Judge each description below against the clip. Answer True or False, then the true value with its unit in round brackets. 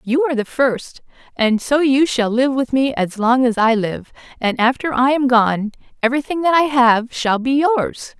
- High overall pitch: True (255 Hz)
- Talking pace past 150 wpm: True (205 wpm)